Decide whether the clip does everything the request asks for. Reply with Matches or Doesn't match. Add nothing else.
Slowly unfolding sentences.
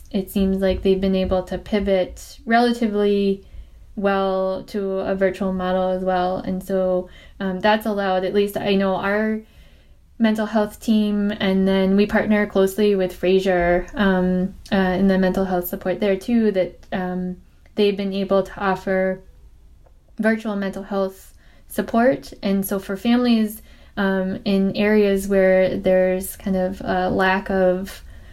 Doesn't match